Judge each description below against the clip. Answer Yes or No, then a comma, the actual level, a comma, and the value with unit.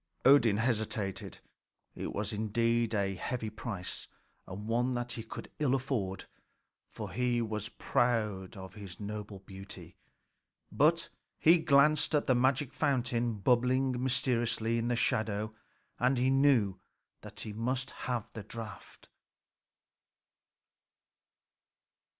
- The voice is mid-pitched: No, low, 115 Hz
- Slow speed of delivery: Yes, slow, 120 wpm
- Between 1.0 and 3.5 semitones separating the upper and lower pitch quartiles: Yes, average, 3.2 semitones